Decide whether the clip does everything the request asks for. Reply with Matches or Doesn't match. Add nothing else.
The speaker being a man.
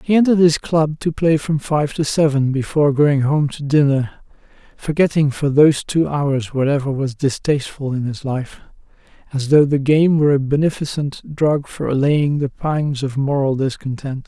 Matches